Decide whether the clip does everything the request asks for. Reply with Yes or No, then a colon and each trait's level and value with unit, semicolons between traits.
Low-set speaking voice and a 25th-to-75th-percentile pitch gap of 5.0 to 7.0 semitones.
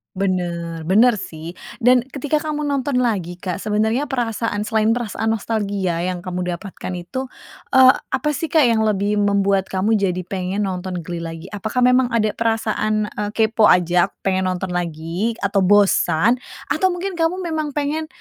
No: high, 210 Hz; wide, 5.4 semitones